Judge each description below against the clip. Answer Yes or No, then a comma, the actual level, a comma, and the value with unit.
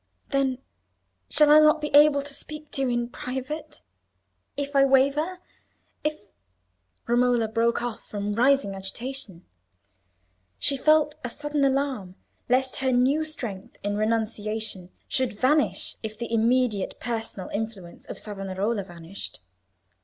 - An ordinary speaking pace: No, slow, 130 wpm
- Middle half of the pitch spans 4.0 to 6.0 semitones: Yes, average, 4.7 semitones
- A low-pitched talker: No, high, 245 Hz